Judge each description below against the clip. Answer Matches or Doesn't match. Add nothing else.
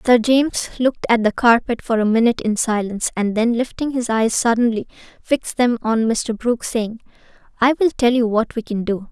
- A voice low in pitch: Doesn't match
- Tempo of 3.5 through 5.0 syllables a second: Doesn't match